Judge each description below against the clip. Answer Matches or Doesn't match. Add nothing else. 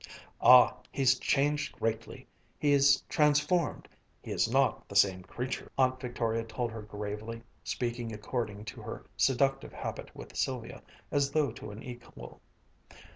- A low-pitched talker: Matches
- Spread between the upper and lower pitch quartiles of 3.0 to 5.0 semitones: Matches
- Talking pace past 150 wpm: Doesn't match